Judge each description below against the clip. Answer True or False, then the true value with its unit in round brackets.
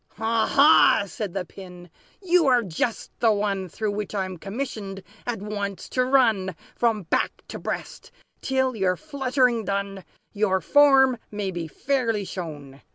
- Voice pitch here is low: False (210 Hz)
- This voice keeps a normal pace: True (150 wpm)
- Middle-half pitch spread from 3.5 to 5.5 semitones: True (4.8 semitones)